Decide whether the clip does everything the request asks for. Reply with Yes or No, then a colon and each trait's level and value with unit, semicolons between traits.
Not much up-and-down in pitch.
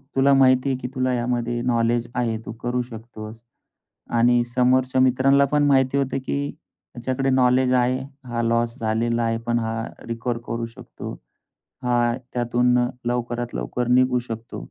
Yes: narrow, 1.6 semitones